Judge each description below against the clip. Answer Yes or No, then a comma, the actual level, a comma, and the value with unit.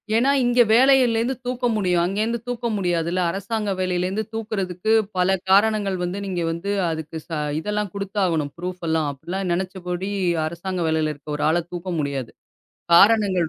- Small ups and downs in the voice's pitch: No, average, 3.8 semitones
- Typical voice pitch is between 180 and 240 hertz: Yes, medium, 185 Hz